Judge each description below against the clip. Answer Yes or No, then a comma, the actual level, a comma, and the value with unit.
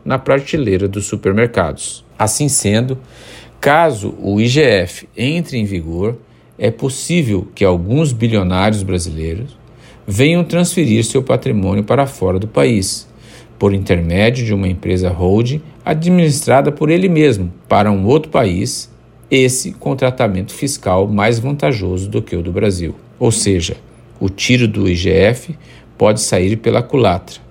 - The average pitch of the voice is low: Yes, low, 110 Hz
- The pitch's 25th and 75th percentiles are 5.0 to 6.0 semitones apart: Yes, wide, 5.4 semitones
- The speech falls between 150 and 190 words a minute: No, average, 135 wpm